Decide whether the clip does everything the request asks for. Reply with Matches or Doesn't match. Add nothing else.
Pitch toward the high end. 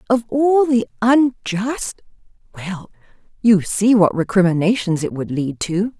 Matches